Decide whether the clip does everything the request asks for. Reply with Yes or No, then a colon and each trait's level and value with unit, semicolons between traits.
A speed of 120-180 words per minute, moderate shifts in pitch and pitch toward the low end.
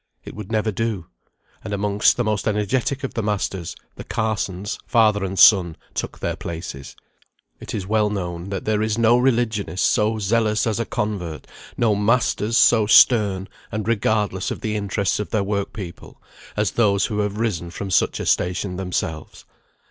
No: average, 170 wpm; narrow, 2.3 semitones; low, 105 Hz